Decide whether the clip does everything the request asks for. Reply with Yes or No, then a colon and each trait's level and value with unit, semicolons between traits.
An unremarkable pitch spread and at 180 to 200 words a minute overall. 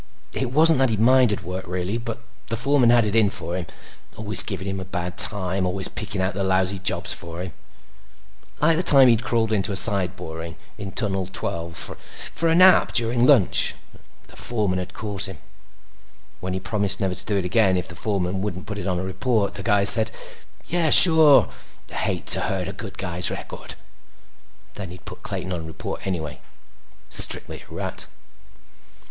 Yes: average, 3.8 semitones; average, 185 wpm